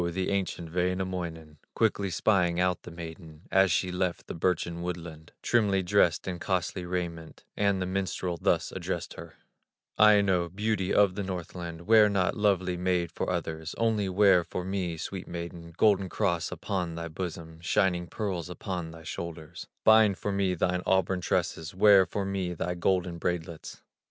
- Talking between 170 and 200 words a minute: No, average, 160 wpm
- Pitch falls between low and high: No, very low, 90 Hz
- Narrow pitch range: Yes, narrow, 2.3 semitones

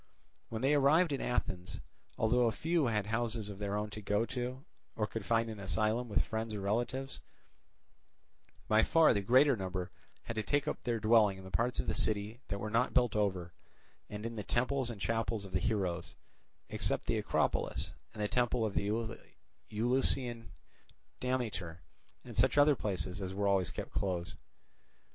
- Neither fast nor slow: Yes, average, 180 wpm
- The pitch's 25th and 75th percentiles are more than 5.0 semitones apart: No, average, 3.3 semitones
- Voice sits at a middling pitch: No, low, 110 Hz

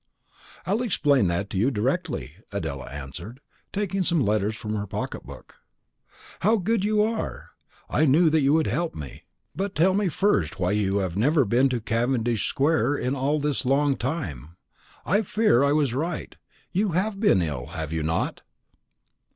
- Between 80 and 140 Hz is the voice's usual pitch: Yes, low, 135 Hz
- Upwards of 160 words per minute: Yes, average, 170 wpm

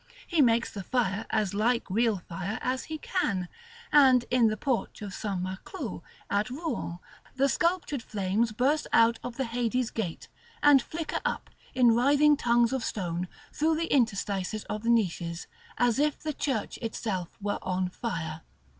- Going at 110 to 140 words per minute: No, average, 165 wpm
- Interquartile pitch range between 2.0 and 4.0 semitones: No, average, 4.9 semitones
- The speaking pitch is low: No, high, 230 Hz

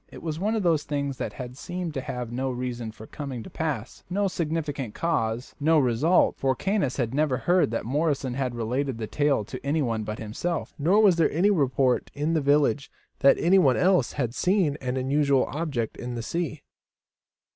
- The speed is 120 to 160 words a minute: No, average, 190 wpm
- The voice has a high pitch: No, medium, 140 Hz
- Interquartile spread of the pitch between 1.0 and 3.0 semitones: No, average, 4.7 semitones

